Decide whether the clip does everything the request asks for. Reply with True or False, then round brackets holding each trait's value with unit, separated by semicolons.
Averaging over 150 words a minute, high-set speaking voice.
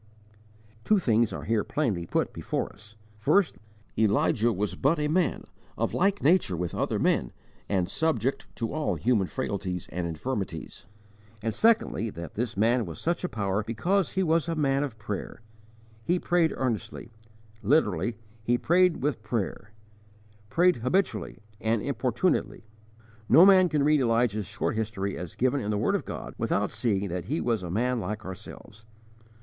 False (165 wpm; 115 Hz)